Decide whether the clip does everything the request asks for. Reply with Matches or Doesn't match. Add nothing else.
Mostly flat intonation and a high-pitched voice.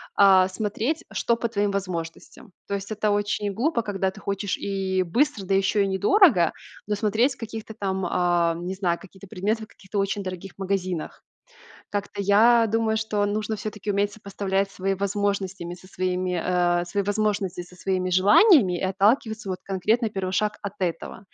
Matches